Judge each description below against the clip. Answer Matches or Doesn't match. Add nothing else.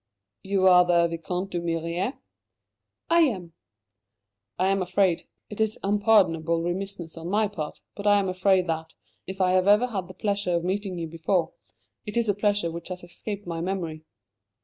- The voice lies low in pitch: Doesn't match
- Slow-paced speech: Doesn't match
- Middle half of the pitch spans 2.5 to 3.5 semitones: Matches